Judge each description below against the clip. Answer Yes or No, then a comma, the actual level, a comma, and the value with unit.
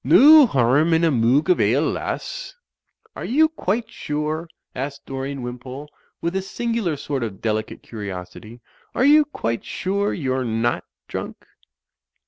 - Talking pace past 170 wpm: No, average, 140 wpm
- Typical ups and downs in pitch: No, wide, 8.2 semitones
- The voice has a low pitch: No, medium, 145 Hz